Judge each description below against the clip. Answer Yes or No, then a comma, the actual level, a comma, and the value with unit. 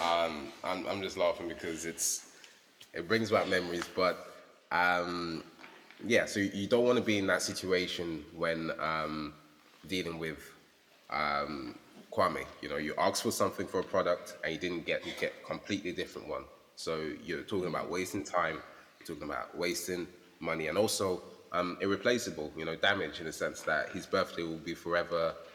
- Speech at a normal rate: Yes, average, 175 wpm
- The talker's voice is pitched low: Yes, very low, 85 Hz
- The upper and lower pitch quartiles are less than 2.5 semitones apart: Yes, narrow, 1.8 semitones